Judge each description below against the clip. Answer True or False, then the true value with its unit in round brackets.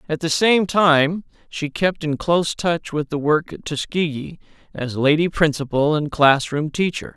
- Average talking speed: True (170 wpm)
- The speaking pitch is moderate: True (160 Hz)